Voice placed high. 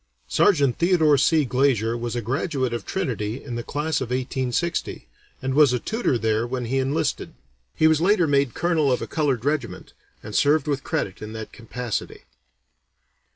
No: low, 135 Hz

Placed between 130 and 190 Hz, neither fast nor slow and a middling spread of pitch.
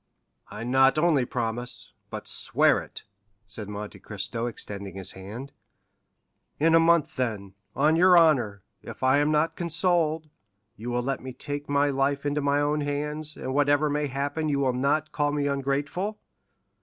Yes: medium, 140 Hz; average, 165 wpm; average, 3.7 semitones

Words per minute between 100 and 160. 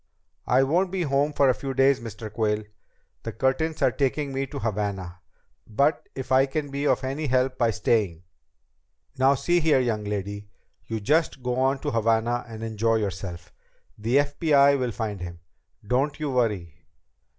No: average, 175 wpm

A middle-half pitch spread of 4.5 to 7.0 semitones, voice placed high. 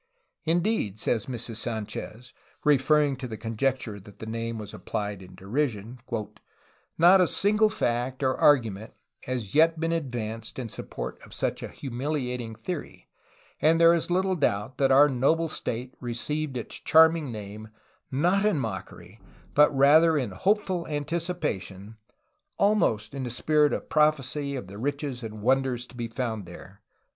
No: wide, 5.6 semitones; low, 130 Hz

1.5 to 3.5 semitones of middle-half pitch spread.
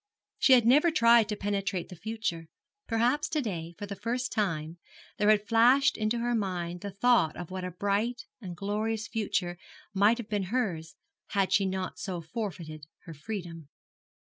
No: average, 4.5 semitones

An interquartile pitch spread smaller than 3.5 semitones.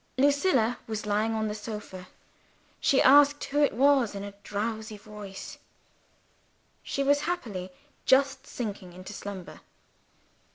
No: average, 5.2 semitones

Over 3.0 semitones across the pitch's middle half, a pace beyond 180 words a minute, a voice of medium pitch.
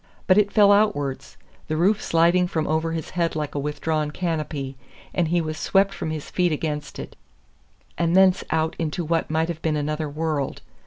No: narrow, 2.4 semitones; average, 190 wpm; medium, 160 Hz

